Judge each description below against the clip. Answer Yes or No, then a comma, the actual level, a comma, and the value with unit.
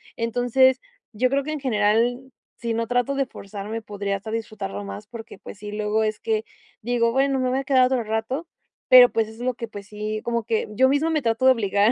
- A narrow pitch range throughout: No, average, 3.1 semitones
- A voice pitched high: Yes, high, 230 Hz